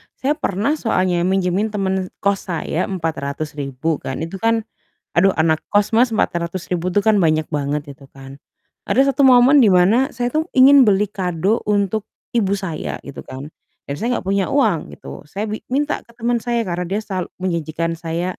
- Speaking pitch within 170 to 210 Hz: Yes, high, 190 Hz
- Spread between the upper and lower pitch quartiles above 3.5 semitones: Yes, average, 4.9 semitones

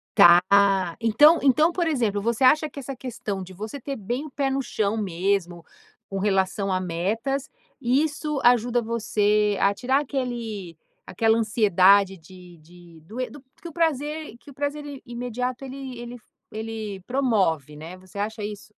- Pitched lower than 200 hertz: No, high, 225 Hz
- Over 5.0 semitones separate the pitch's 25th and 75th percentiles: Yes, wide, 5.4 semitones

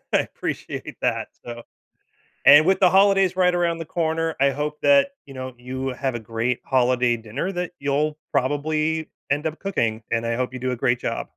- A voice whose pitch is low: No, medium, 145 Hz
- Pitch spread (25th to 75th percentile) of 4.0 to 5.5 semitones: Yes, average, 4.8 semitones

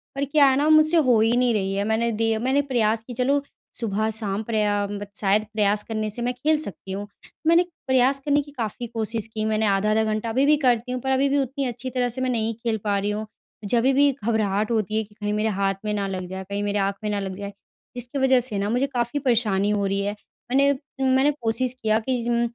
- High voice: Yes, high, 225 Hz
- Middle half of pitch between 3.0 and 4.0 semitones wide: Yes, average, 3.7 semitones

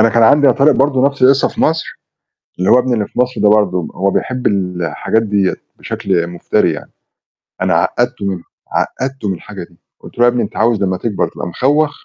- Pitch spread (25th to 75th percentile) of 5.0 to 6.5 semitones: Yes, wide, 5.4 semitones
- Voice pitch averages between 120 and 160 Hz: No, low, 110 Hz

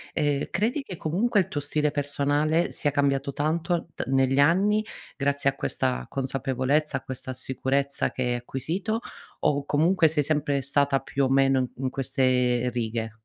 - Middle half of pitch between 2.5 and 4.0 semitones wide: Yes, average, 2.8 semitones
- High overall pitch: No, medium, 140 Hz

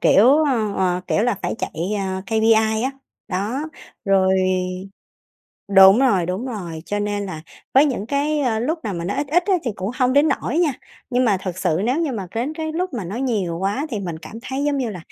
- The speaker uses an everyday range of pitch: No, wide, 5.9 semitones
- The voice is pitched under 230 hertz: Yes, high, 220 Hz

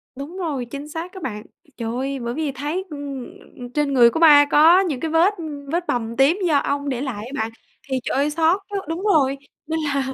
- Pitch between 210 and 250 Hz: No, very high, 285 Hz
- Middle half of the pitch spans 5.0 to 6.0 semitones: No, average, 3.5 semitones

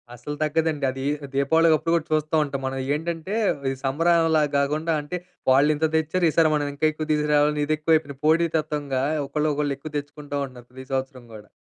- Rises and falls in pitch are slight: Yes, narrow, 2.2 semitones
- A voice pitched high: No, medium, 150 Hz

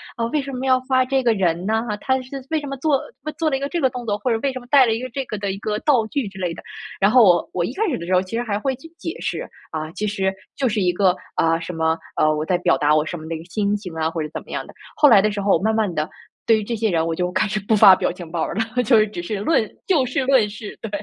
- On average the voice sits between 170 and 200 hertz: No, high, 215 Hz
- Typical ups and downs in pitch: No, wide, 6.2 semitones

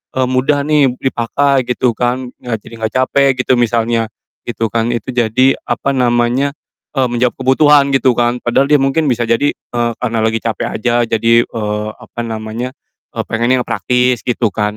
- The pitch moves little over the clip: Yes, narrow, 2.2 semitones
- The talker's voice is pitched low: Yes, low, 120 Hz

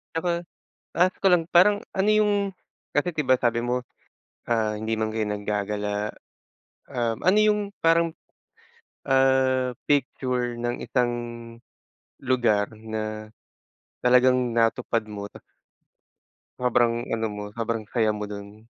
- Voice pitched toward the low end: Yes, low, 120 Hz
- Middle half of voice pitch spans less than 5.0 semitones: Yes, average, 3.7 semitones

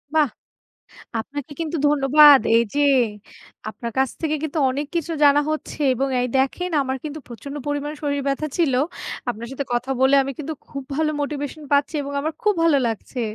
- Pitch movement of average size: No, narrow, 2.3 semitones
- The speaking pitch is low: No, very high, 285 Hz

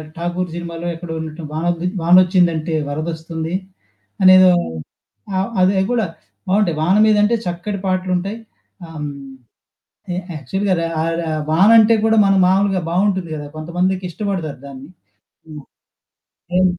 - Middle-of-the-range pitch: Yes, medium, 180 Hz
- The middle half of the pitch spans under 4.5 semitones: Yes, average, 2.8 semitones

